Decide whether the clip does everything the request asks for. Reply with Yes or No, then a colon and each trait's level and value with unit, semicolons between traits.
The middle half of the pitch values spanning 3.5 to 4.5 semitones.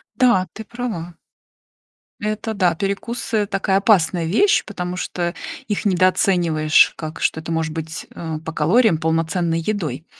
Yes: average, 4.2 semitones